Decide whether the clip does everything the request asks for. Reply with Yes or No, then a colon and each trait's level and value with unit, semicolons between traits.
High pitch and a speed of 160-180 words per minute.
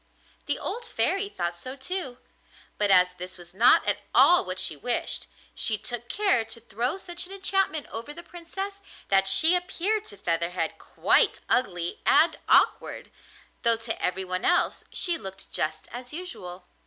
Yes: high, 235 Hz; average, 165 wpm